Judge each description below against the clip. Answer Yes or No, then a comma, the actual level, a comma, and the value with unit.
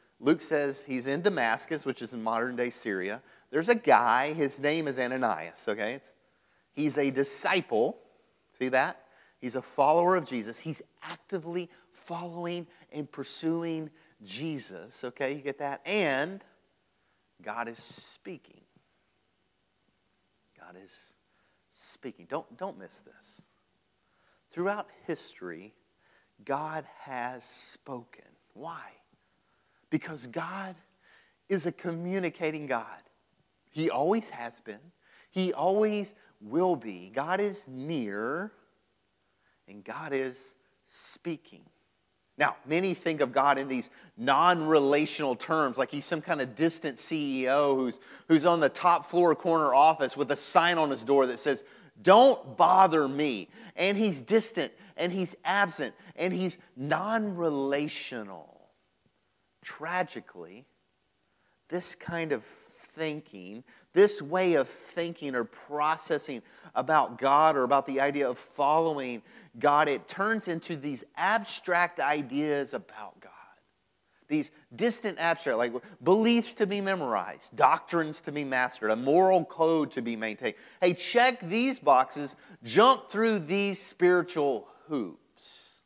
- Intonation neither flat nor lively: Yes, average, 4.7 semitones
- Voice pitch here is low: No, medium, 155 Hz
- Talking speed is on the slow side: Yes, slow, 125 wpm